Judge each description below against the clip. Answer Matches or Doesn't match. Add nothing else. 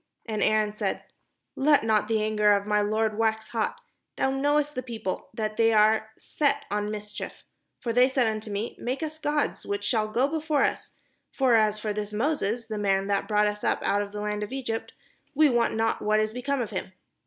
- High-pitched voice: Matches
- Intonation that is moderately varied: Matches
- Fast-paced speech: Matches